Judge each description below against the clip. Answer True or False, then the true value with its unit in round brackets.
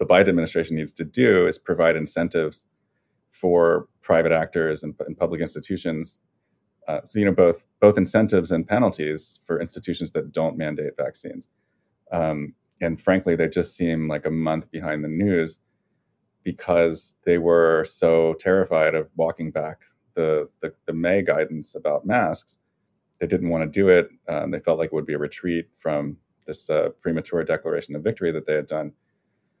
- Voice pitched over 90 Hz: False (80 Hz)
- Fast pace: False (170 wpm)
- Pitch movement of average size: False (1.7 semitones)